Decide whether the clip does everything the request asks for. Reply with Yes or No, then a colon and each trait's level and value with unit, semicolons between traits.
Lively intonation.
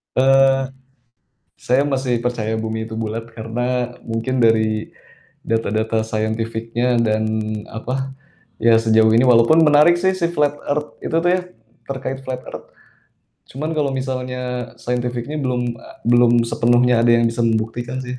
No: average, 2.9 semitones